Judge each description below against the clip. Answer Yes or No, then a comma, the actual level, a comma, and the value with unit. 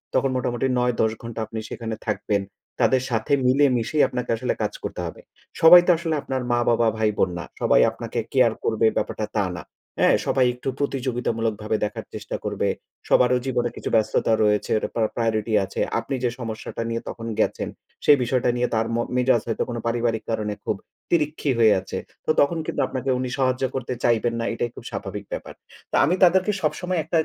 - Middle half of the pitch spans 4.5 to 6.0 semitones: No, average, 2.9 semitones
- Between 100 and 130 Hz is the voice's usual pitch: Yes, low, 120 Hz